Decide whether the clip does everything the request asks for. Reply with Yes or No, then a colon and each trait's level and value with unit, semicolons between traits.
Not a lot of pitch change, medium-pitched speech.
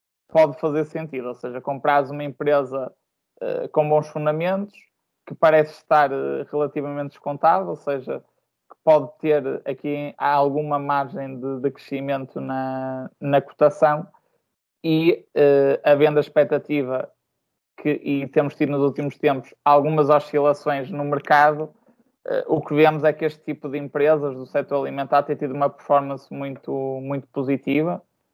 Yes: narrow, 1.6 semitones; medium, 145 Hz